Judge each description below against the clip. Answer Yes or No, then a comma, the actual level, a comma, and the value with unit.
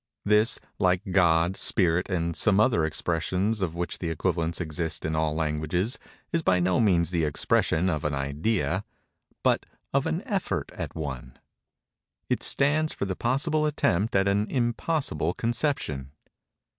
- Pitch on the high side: No, very low, 90 Hz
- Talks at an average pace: Yes, average, 145 wpm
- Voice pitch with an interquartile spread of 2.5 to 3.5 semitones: No, average, 5.2 semitones